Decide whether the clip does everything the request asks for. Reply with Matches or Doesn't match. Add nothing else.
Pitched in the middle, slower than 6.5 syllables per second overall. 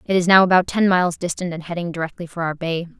Doesn't match